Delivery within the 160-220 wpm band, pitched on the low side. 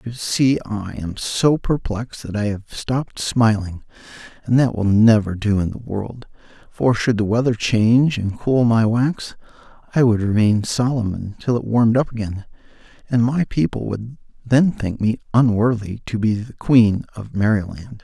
Yes: average, 170 wpm; low, 115 Hz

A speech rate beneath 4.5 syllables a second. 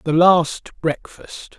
Yes: 3.0 syllables/s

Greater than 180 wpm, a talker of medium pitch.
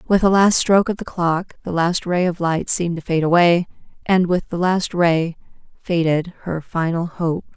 Yes: average, 200 wpm; medium, 175 Hz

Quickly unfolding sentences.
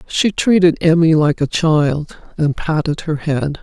No: average, 165 wpm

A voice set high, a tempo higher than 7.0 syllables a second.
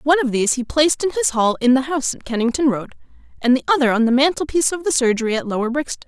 Yes: very high, 265 Hz; 7.6 syllables/s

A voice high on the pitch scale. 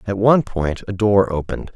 No: low, 100 Hz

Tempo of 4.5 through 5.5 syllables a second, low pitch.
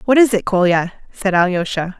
No: 5.4 syllables/s; high, 195 Hz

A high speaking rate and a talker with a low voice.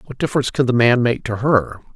Yes: fast, 245 wpm; low, 125 Hz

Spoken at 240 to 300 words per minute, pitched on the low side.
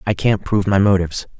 No: fast, 215 wpm; very low, 95 Hz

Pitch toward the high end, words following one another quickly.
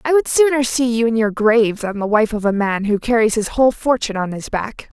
Yes: high, 230 Hz; fast, 265 wpm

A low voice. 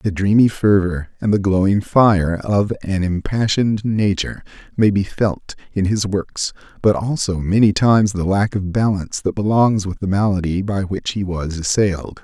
Yes: low, 100 Hz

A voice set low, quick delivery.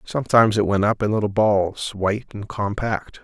No: low, 105 Hz; average, 185 wpm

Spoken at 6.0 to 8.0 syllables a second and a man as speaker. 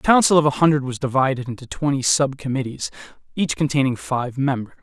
Yes: 6.1 syllables/s; male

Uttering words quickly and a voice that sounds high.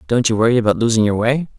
No: fast, 265 wpm; low, 115 Hz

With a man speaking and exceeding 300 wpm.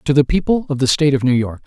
Yes: male; fast, 325 wpm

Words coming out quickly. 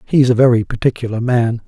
No: average, 180 wpm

